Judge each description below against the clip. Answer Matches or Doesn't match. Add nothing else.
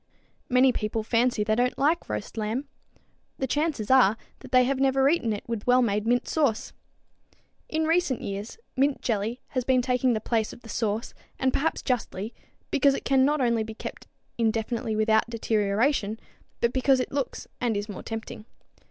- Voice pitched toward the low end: Doesn't match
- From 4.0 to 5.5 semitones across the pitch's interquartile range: Doesn't match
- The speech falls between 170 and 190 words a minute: Matches